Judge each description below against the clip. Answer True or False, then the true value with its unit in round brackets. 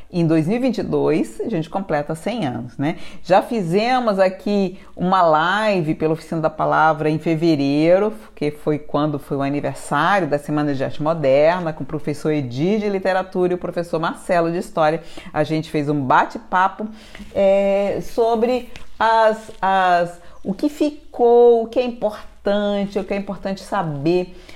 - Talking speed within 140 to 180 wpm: True (155 wpm)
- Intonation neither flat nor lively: True (4.7 semitones)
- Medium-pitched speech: True (180 Hz)